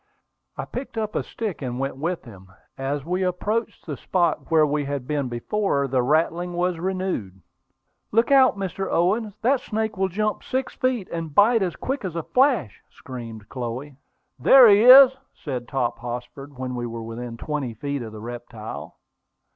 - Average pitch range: No, wide, 8.6 semitones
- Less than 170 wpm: No, average, 175 wpm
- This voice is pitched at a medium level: Yes, medium, 155 Hz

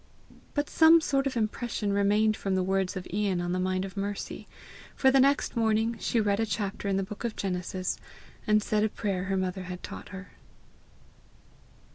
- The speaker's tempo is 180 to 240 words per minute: Yes, average, 190 wpm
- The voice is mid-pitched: No, high, 200 Hz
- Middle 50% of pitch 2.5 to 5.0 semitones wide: Yes, average, 2.9 semitones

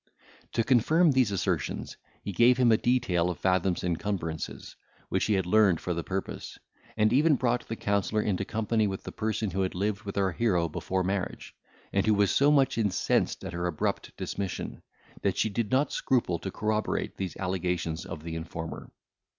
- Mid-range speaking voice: No, low, 100 Hz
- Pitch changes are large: No, average, 3.9 semitones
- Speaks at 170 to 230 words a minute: Yes, average, 185 wpm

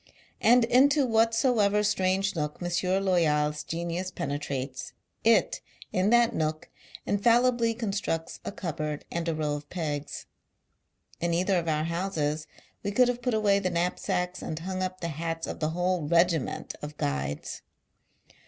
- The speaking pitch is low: No, medium, 180 Hz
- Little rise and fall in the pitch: No, average, 4.6 semitones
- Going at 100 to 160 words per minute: Yes, average, 155 wpm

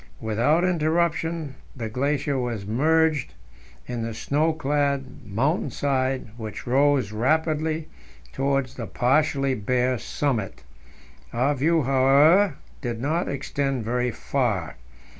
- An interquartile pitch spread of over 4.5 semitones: No, average, 3.8 semitones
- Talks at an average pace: No, slow, 110 wpm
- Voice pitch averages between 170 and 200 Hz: No, low, 135 Hz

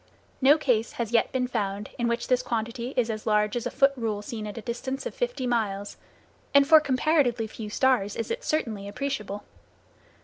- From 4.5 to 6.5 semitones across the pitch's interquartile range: No, average, 3.7 semitones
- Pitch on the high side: Yes, high, 235 Hz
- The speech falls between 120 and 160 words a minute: No, average, 195 wpm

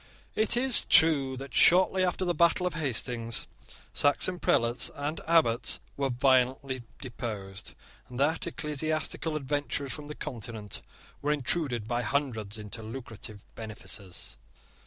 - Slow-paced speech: Yes, slow, 125 wpm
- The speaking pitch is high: No, low, 135 Hz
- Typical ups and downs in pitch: Yes, average, 5.0 semitones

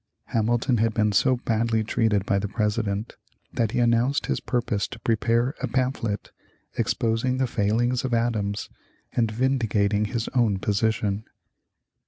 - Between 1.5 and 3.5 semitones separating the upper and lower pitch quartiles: Yes, narrow, 2.5 semitones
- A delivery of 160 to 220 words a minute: No, average, 140 wpm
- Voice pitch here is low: Yes, low, 115 Hz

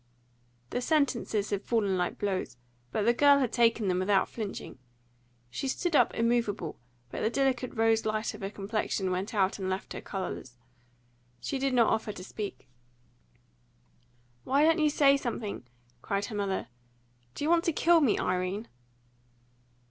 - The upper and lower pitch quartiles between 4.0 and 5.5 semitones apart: Yes, average, 5.0 semitones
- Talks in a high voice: Yes, high, 220 Hz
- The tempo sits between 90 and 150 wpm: No, average, 160 wpm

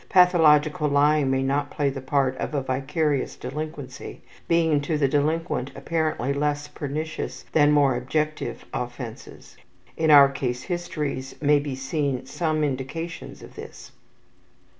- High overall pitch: No, medium, 145 Hz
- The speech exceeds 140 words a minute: No, slow, 135 wpm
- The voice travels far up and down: No, narrow, 2.5 semitones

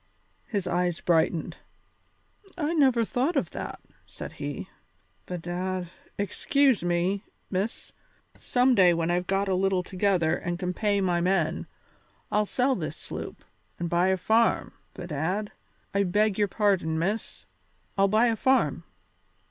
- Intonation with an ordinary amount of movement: Yes, average, 3.5 semitones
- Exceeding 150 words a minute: No, average, 140 wpm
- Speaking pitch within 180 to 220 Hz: Yes, high, 190 Hz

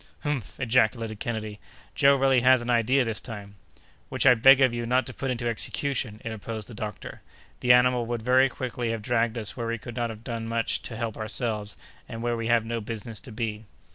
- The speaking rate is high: Yes, fast, 210 wpm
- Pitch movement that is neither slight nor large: No, narrow, 2.0 semitones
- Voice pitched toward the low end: Yes, low, 115 Hz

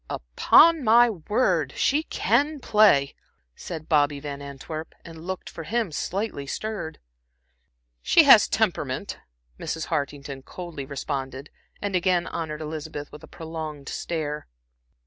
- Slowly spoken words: Yes, slow, 125 wpm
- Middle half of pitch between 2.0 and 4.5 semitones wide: No, wide, 5.4 semitones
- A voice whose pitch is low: No, medium, 160 Hz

